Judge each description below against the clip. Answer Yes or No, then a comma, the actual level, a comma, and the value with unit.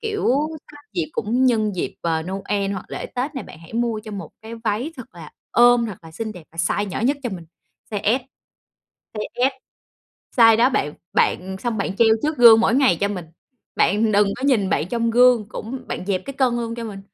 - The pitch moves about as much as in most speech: Yes, average, 3.8 semitones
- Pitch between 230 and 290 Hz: No, high, 220 Hz